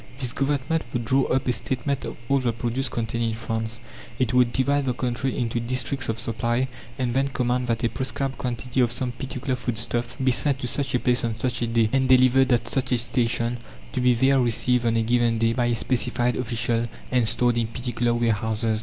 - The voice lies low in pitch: Yes, low, 120 Hz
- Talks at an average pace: No, fast, 215 wpm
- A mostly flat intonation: Yes, narrow, 1.9 semitones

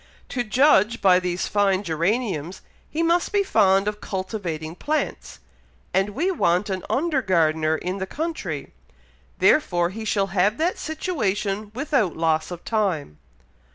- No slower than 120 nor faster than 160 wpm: Yes, average, 140 wpm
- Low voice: No, high, 200 Hz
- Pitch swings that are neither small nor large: No, wide, 6.0 semitones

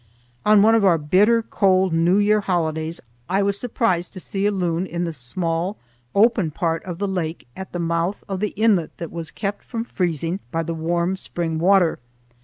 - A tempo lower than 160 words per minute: No, average, 195 wpm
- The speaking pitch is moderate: Yes, medium, 180 Hz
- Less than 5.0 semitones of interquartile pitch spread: Yes, average, 3.3 semitones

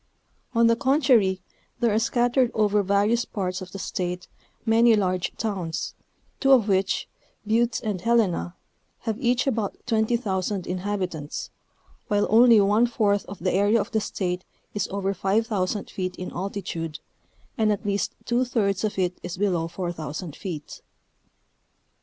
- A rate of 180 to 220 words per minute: No, average, 145 wpm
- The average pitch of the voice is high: Yes, high, 205 Hz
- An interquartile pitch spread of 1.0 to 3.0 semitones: No, average, 3.6 semitones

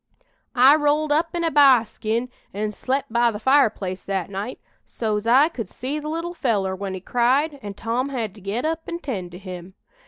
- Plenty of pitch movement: Yes, wide, 6.1 semitones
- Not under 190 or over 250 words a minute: Yes, fast, 205 wpm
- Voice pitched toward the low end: No, high, 240 Hz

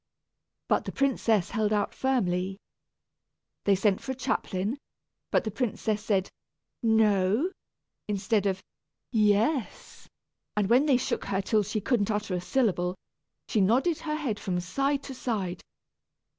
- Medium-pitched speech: No, high, 215 Hz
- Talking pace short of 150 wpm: Yes, average, 140 wpm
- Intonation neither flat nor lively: Yes, average, 4.6 semitones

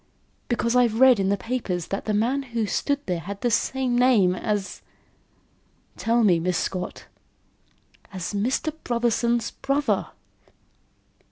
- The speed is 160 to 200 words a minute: No, average, 140 wpm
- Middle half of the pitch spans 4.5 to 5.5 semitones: No, average, 4.1 semitones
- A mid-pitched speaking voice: No, high, 230 Hz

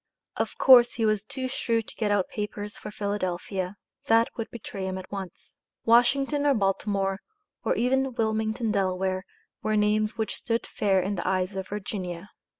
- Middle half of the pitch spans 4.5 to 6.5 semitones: No, average, 3.1 semitones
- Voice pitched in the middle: No, high, 210 Hz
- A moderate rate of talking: Yes, average, 165 wpm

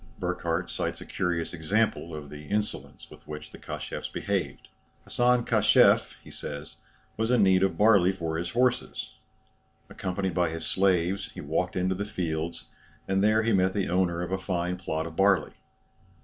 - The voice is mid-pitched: No, very low, 95 Hz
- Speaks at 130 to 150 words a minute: No, average, 165 wpm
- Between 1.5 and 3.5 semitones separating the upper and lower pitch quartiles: Yes, average, 3.1 semitones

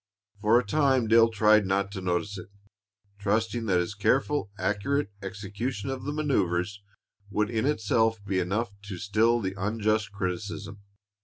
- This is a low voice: Yes, low, 105 Hz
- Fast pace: No, average, 150 wpm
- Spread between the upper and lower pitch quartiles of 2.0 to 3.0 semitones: Yes, narrow, 2.5 semitones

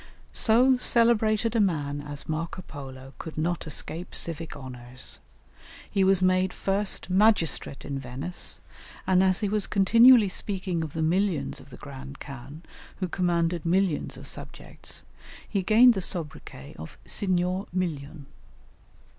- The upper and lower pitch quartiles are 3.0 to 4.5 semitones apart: No, average, 5.2 semitones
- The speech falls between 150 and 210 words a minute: No, average, 140 wpm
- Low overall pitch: No, medium, 175 Hz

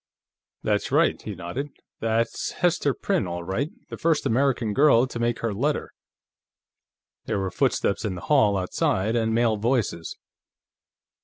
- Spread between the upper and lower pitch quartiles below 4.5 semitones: No, average, 5.2 semitones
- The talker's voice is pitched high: No, low, 115 Hz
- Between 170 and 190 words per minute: No, average, 145 wpm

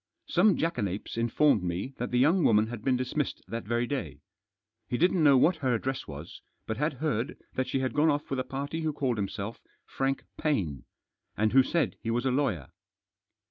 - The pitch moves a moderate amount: Yes, average, 4.7 semitones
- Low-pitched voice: Yes, low, 130 Hz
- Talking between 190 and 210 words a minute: Yes, average, 195 wpm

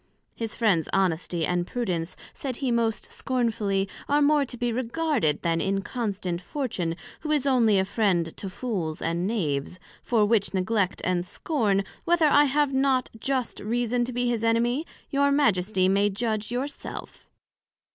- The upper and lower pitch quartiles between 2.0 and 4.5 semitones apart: No, wide, 5.4 semitones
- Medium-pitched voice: No, high, 225 Hz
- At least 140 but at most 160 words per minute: Yes, average, 155 wpm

